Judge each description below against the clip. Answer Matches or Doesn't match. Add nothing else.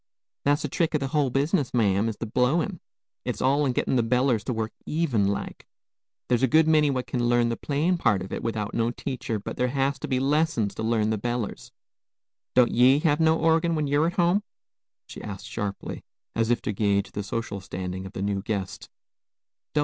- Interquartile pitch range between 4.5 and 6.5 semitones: Matches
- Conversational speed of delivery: Doesn't match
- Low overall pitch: Matches